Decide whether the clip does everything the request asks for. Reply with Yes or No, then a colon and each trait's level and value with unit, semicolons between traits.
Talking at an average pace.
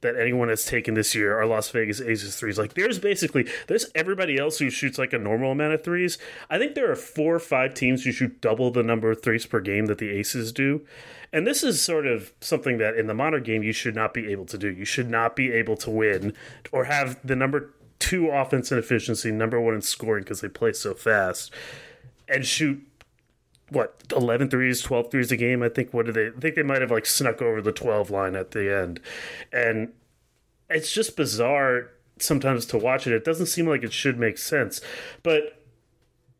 No: fast, 220 wpm